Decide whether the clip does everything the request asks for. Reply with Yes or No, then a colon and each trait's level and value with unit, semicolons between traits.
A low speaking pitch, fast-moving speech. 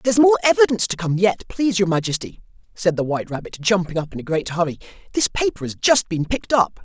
No: high, 195 Hz; fast, 230 wpm